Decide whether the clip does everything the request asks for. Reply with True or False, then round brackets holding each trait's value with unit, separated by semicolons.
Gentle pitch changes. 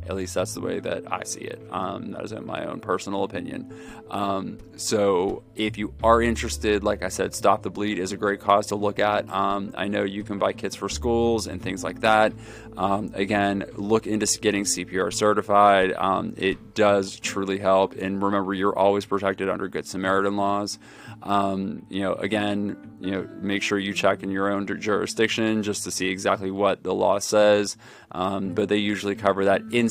True (1.4 semitones)